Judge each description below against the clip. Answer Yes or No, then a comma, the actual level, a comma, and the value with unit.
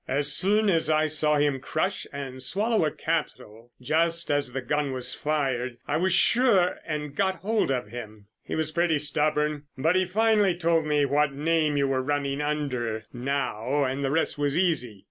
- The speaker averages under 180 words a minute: No, average, 185 wpm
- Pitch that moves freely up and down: No, average, 3.6 semitones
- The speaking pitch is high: No, medium, 150 Hz